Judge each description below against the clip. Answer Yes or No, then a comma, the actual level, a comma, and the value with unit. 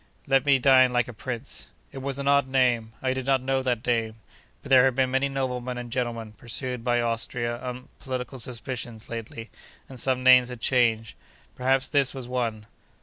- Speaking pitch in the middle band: No, low, 125 Hz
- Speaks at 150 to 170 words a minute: No, average, 190 wpm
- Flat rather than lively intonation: Yes, narrow, 1.9 semitones